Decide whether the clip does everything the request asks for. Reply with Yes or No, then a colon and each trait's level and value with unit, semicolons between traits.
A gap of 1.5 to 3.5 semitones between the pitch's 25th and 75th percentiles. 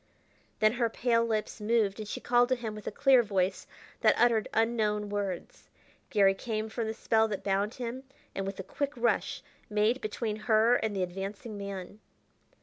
Yes: narrow, 2.5 semitones